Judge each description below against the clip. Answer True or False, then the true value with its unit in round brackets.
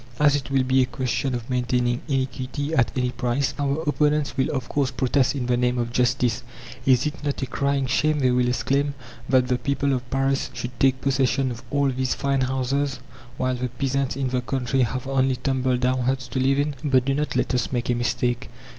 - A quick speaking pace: True (215 wpm)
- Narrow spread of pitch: True (1.7 semitones)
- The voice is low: True (130 Hz)